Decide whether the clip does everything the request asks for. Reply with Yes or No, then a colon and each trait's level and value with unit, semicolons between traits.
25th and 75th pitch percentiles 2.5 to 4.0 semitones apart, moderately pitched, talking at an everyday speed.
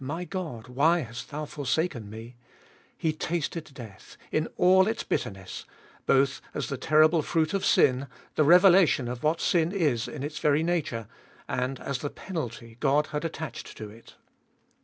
No: average, 4.7 semitones; medium, 150 Hz; average, 165 wpm